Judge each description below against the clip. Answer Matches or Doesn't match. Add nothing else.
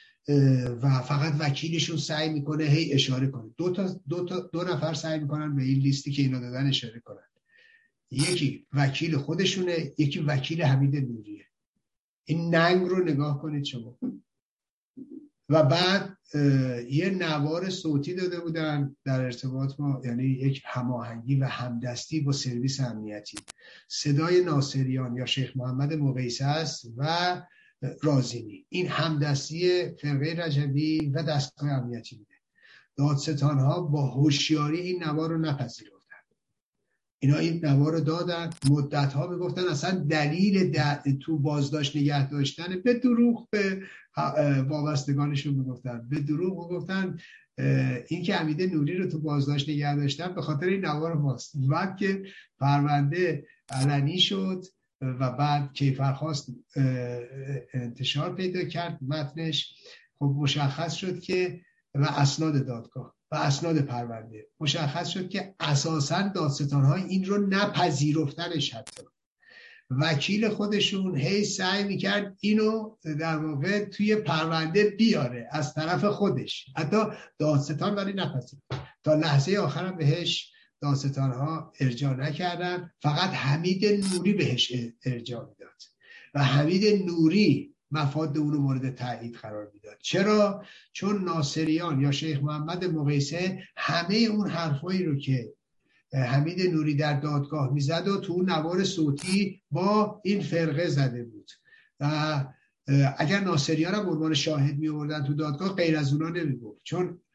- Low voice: Doesn't match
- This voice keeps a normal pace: Matches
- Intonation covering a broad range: Doesn't match